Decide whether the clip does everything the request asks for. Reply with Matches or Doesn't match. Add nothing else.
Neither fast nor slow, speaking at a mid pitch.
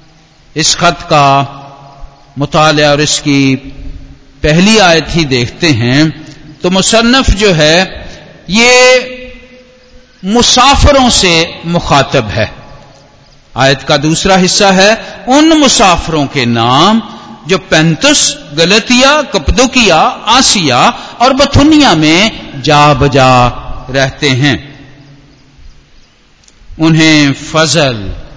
Doesn't match